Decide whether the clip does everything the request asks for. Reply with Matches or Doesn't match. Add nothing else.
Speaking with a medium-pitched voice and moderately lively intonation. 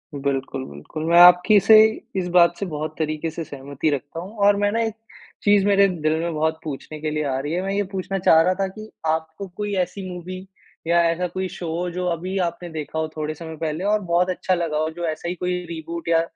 Matches